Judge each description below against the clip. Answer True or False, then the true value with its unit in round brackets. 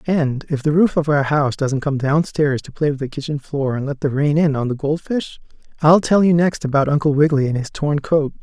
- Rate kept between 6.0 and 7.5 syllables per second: False (5.5 syllables/s)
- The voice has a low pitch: False (145 Hz)